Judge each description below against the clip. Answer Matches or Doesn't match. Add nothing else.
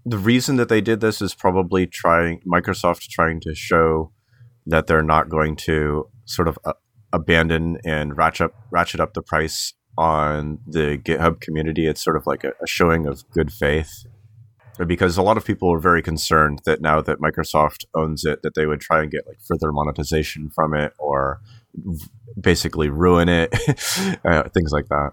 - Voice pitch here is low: Matches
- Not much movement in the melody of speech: Doesn't match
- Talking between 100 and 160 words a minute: Doesn't match